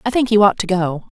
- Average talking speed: No, fast, 315 wpm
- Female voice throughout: Yes, female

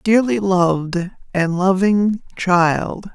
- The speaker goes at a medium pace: No, slow, 95 wpm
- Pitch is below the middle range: No, medium, 185 Hz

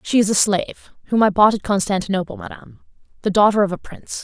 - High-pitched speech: Yes, high, 200 Hz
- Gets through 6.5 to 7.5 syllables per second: Yes, 6.7 syllables/s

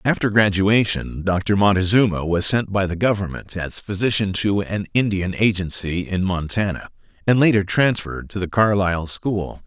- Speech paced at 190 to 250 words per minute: No, average, 150 wpm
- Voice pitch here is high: No, low, 100 Hz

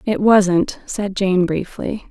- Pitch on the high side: Yes, high, 195 Hz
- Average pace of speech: Yes, average, 145 wpm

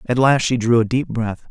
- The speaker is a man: Yes, male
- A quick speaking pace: Yes, fast, 280 wpm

